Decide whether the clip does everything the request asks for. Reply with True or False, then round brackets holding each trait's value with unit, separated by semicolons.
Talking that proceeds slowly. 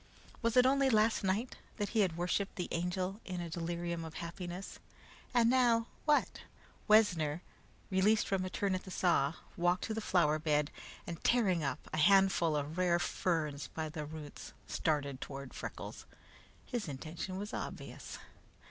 False (160 wpm)